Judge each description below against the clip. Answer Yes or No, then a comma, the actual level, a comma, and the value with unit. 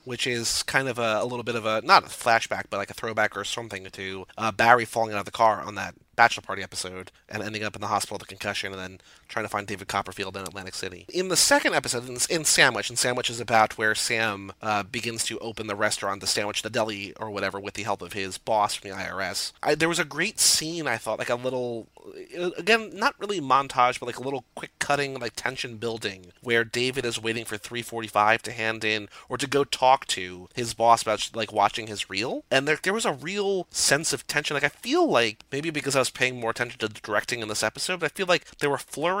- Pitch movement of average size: Yes, average, 4.5 semitones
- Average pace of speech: No, fast, 250 wpm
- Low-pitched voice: Yes, low, 115 Hz